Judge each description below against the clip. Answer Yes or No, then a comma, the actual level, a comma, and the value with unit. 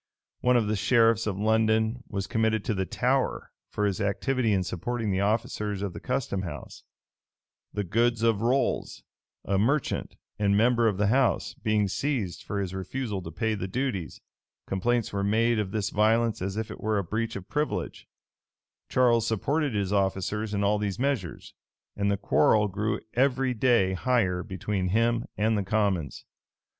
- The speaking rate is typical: Yes, average, 170 wpm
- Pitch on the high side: No, low, 105 Hz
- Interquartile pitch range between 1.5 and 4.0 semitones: Yes, average, 3.0 semitones